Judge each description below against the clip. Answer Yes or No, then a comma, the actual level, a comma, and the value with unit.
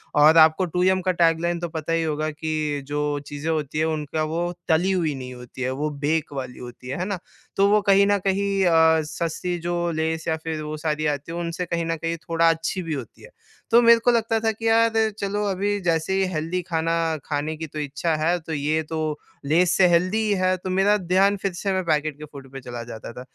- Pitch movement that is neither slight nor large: Yes, average, 3.3 semitones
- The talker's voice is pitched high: No, medium, 165 Hz